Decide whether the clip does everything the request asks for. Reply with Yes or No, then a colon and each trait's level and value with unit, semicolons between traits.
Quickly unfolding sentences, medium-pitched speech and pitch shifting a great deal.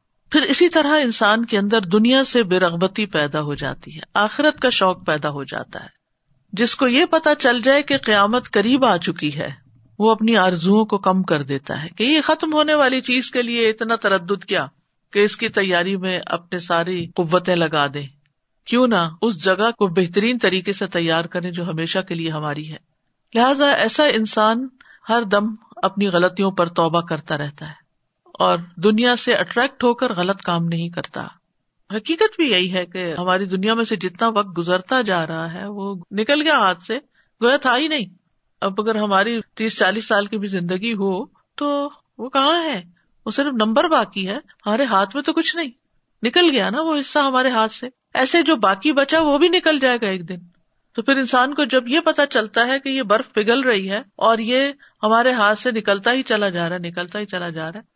No: fast, 205 wpm; high, 210 Hz; wide, 6.0 semitones